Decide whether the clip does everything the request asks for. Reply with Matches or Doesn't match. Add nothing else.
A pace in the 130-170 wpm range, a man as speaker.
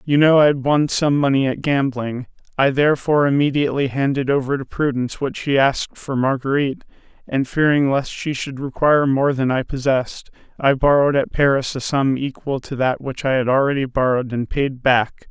Doesn't match